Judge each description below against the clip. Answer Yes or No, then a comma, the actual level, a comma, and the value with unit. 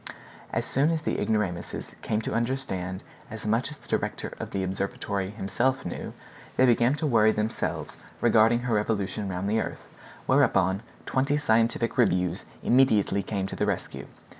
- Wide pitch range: No, average, 3.7 semitones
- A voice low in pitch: Yes, low, 110 Hz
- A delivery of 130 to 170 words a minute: Yes, average, 160 wpm